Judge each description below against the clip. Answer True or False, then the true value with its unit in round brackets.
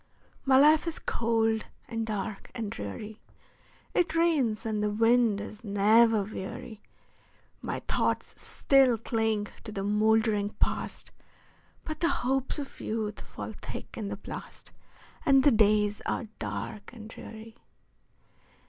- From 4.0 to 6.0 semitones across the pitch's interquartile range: False (2.7 semitones)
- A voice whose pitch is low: False (220 Hz)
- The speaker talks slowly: True (130 wpm)